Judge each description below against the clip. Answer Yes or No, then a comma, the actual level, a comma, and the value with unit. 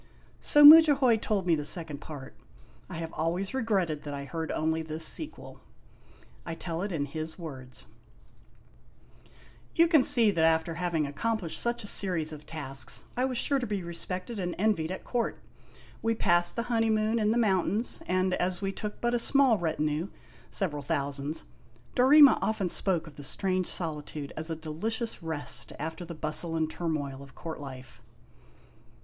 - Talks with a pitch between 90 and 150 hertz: No, medium, 170 Hz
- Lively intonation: Yes, wide, 5.8 semitones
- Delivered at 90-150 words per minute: No, average, 165 wpm